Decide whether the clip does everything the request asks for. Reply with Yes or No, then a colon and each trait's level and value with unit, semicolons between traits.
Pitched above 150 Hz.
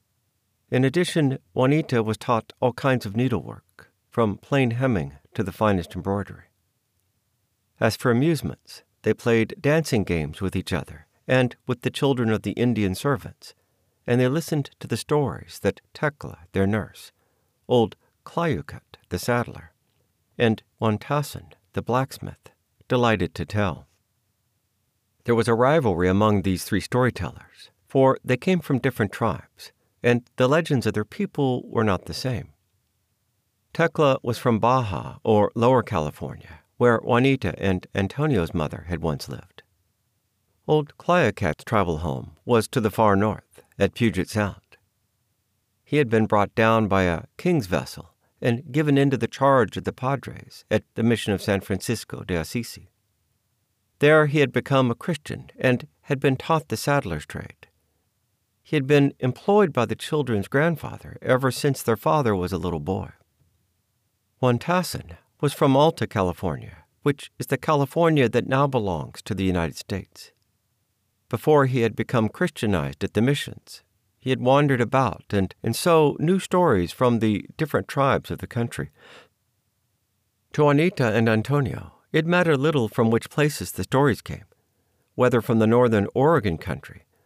No: low, 115 Hz